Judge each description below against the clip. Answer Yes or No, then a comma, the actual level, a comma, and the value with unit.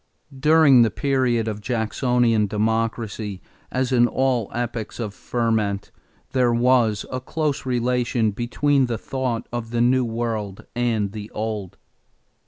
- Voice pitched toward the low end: Yes, low, 120 Hz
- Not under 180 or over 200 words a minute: No, slow, 135 wpm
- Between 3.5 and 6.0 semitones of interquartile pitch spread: No, narrow, 2.5 semitones